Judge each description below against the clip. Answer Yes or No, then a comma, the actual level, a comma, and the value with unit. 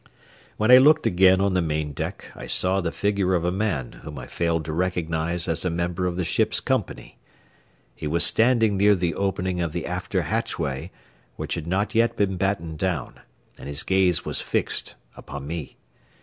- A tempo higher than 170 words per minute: Yes, average, 190 wpm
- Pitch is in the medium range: No, very low, 90 Hz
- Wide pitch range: No, average, 3.2 semitones